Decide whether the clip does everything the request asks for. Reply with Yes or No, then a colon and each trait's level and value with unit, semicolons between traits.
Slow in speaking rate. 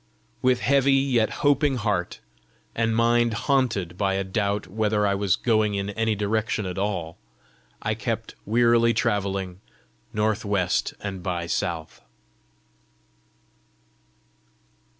Yes: slow, 115 wpm